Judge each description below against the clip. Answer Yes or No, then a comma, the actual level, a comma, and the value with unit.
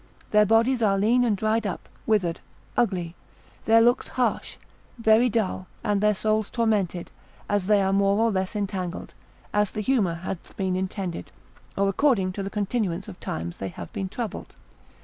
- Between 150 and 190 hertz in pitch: No, high, 205 Hz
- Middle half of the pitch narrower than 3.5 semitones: Yes, average, 2.9 semitones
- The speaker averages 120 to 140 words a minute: No, average, 170 wpm